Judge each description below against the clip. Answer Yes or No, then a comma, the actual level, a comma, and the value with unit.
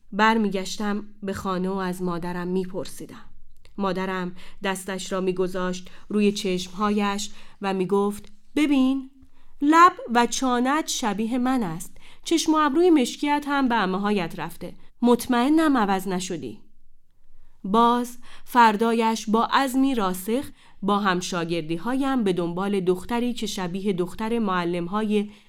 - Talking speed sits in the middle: Yes, average, 120 wpm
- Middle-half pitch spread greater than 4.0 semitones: Yes, average, 4.6 semitones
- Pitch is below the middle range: No, high, 205 Hz